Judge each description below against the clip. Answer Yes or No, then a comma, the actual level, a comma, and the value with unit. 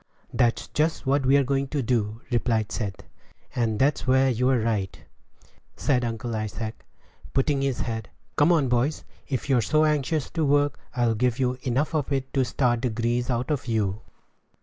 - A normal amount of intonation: Yes, average, 3.1 semitones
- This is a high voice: No, low, 125 Hz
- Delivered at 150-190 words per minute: Yes, average, 175 wpm